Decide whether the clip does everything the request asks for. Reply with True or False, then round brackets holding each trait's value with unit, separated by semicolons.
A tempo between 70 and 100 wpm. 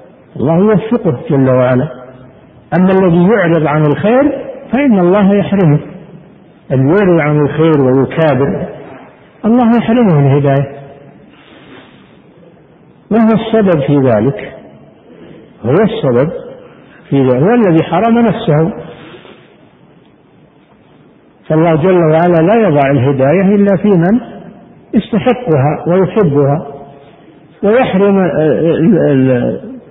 True (90 wpm)